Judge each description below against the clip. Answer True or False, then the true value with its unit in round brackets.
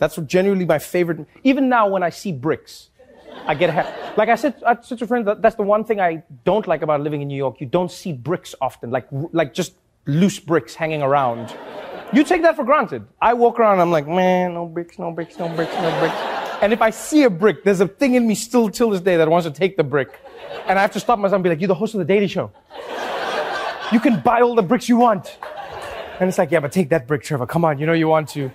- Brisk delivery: True (260 wpm)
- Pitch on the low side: False (185 Hz)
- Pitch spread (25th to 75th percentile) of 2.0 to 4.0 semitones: False (5.6 semitones)